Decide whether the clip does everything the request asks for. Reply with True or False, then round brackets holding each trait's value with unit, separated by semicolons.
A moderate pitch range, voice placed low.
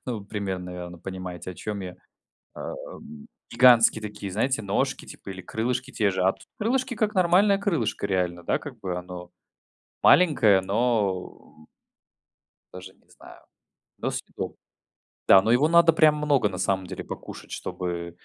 False (6.3 semitones; 100 Hz)